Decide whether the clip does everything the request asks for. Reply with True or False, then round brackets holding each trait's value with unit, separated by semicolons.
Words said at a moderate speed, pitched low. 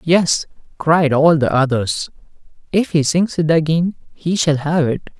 False (160 wpm; 155 Hz)